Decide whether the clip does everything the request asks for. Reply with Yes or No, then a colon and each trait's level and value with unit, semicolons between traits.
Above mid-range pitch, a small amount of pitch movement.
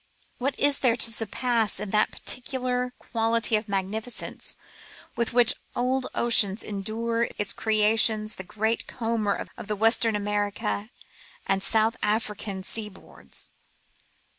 Yes: high, 220 Hz; narrow, 2.1 semitones